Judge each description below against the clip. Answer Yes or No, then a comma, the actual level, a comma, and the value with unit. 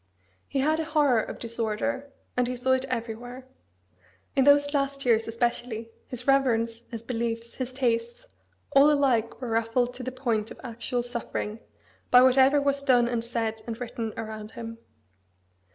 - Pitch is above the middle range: Yes, high, 245 Hz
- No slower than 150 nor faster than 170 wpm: Yes, average, 160 wpm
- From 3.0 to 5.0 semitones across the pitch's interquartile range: No, narrow, 2.6 semitones